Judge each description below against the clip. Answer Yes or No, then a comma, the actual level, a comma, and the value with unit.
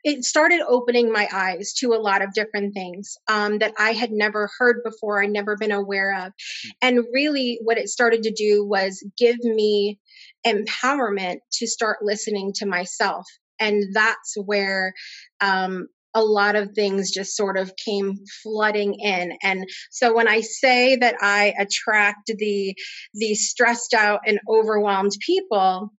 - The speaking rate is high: No, average, 155 wpm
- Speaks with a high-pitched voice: Yes, high, 210 Hz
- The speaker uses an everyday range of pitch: No, narrow, 2.3 semitones